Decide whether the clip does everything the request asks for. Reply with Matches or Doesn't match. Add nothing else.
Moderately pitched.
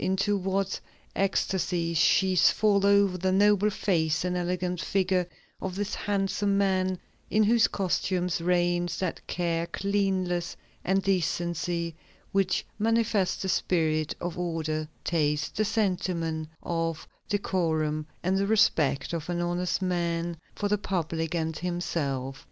Matches